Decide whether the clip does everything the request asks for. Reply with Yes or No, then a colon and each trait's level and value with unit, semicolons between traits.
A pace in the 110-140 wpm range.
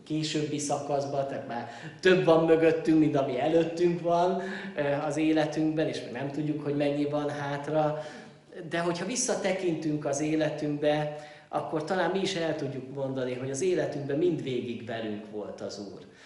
No: average, 150 wpm